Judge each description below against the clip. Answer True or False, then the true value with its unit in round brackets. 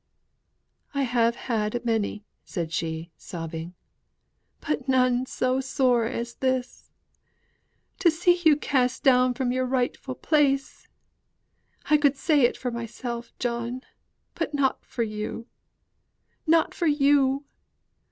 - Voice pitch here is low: False (255 Hz)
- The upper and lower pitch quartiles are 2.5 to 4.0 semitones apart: True (2.9 semitones)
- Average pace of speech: False (125 wpm)